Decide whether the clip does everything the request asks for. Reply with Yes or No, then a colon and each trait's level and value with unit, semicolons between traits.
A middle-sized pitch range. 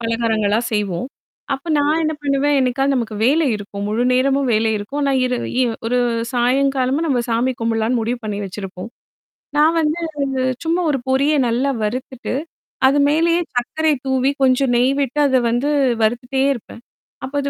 Yes: average, 3.4 semitones